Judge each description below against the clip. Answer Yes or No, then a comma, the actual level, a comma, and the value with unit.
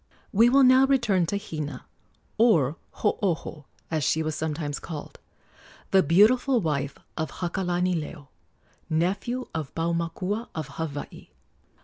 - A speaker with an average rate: No, slow, 115 wpm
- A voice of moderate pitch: Yes, medium, 170 Hz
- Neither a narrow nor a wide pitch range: Yes, average, 5.0 semitones